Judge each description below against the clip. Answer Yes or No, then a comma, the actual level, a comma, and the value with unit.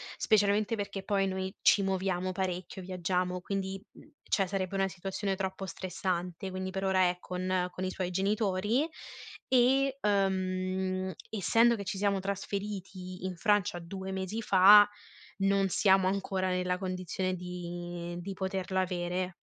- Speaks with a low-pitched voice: No, high, 190 Hz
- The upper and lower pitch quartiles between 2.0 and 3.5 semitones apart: No, narrow, 1.3 semitones